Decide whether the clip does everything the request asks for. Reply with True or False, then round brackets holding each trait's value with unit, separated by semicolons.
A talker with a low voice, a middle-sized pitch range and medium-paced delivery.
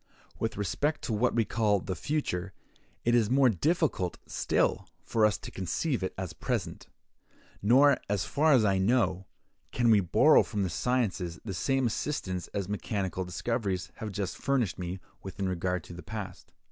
True (105 Hz; 4.7 semitones; 170 wpm)